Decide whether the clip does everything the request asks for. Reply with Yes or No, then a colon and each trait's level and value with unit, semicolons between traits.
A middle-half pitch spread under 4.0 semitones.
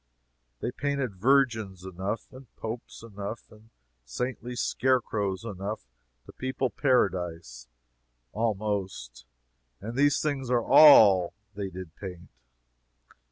No: average, 5.1 semitones